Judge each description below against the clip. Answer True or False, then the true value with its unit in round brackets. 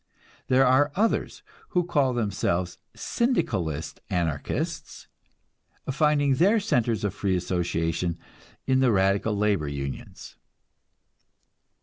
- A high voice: False (105 Hz)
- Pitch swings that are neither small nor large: False (8.4 semitones)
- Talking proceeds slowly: True (95 wpm)